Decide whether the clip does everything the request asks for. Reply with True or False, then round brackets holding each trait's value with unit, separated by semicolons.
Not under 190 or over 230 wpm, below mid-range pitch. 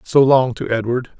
True (200 wpm; 125 Hz)